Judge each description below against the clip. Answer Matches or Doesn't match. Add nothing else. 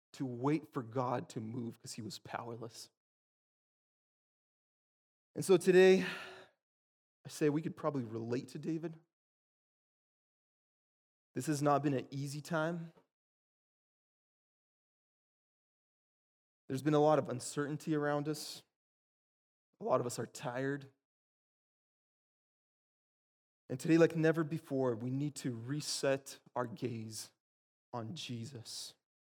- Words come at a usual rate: Doesn't match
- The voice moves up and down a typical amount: Matches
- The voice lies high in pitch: Doesn't match